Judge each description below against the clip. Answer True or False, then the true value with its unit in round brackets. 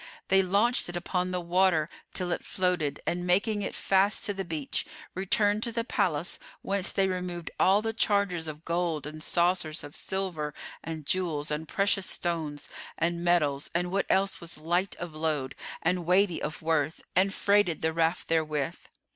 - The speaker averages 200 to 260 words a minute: False (170 wpm)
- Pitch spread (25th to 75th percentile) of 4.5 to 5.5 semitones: False (3.3 semitones)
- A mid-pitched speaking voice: True (175 Hz)